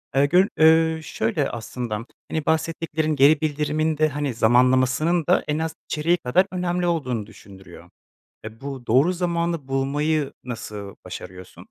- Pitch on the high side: No, medium, 150 Hz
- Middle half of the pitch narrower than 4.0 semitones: No, average, 4.4 semitones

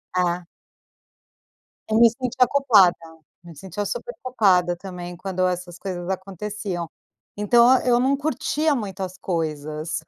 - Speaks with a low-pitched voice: No, high, 190 Hz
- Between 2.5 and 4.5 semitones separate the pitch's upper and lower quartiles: No, average, 5.1 semitones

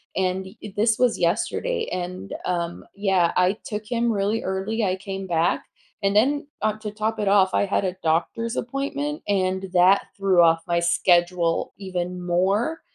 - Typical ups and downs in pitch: Yes, average, 3.2 semitones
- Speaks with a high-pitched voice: Yes, high, 195 Hz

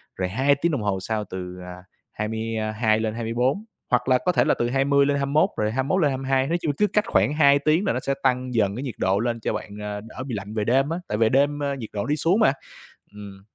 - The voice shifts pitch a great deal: No, average, 4.7 semitones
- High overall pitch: No, low, 125 Hz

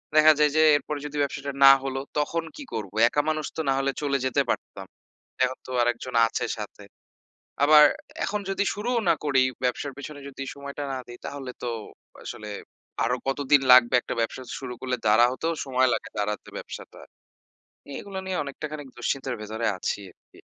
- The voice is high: No, low, 135 Hz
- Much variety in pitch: No, average, 3.2 semitones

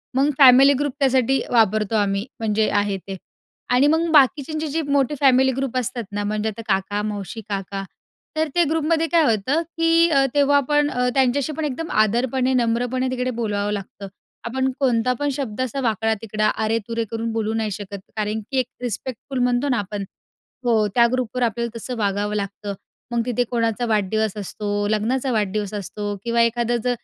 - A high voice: Yes, high, 235 Hz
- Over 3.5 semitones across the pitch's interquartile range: Yes, average, 4.0 semitones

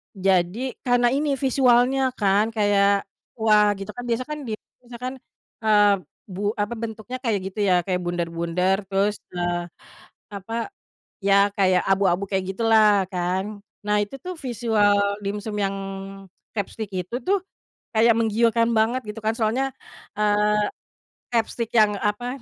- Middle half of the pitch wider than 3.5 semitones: No, average, 3.0 semitones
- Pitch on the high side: Yes, high, 210 Hz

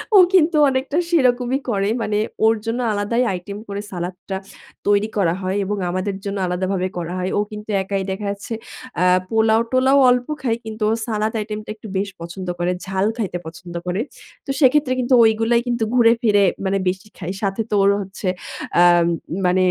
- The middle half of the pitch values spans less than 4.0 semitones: Yes, average, 3.6 semitones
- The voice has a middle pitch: No, high, 205 Hz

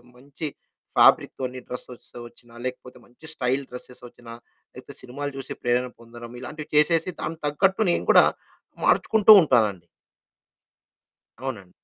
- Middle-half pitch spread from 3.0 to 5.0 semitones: Yes, average, 3.5 semitones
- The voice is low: Yes, low, 125 Hz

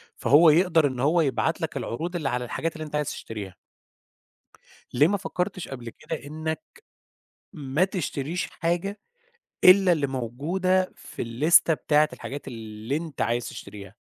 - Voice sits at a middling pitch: Yes, medium, 150 Hz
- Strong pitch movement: Yes, wide, 5.7 semitones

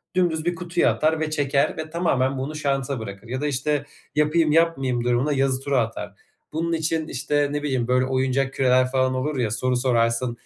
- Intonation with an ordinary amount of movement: Yes, average, 3.2 semitones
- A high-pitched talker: No, low, 135 Hz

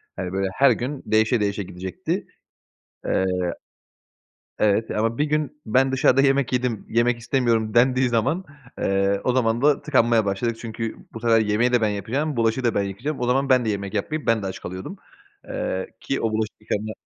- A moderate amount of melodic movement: Yes, average, 3.7 semitones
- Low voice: Yes, low, 115 Hz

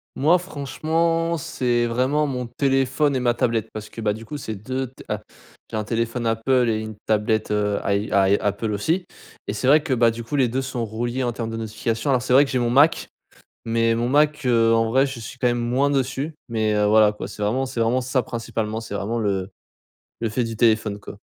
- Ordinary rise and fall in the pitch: Yes, average, 3.3 semitones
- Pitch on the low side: Yes, low, 120 Hz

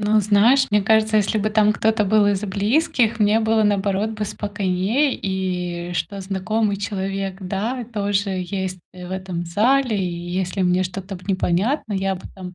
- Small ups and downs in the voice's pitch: Yes, narrow, 2.3 semitones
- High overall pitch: Yes, high, 200 Hz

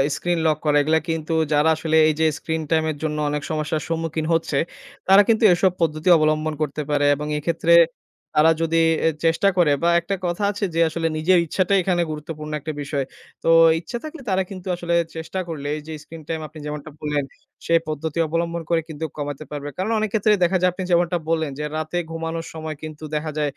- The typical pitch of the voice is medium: Yes, medium, 160 Hz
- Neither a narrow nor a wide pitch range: No, narrow, 2.0 semitones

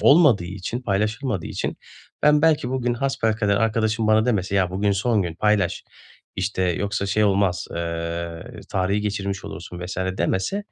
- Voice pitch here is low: Yes, low, 100 Hz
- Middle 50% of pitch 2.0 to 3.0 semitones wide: No, average, 3.4 semitones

